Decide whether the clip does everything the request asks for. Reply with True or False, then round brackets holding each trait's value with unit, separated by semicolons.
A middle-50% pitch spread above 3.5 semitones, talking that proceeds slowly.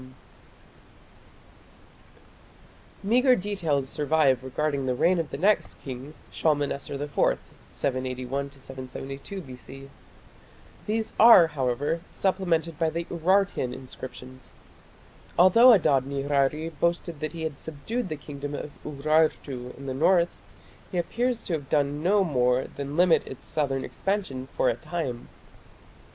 True (4.3 semitones; 120 wpm)